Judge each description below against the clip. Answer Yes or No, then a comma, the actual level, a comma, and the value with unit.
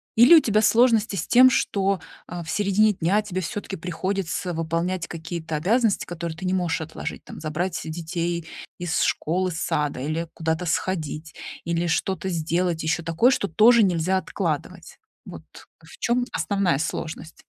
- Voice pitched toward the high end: No, medium, 175 Hz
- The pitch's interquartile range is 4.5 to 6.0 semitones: No, average, 3.5 semitones